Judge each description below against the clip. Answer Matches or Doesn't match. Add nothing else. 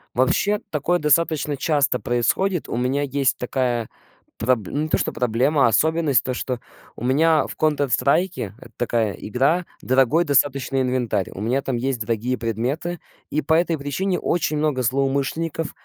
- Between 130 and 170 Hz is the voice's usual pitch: Matches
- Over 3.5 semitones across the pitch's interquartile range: Matches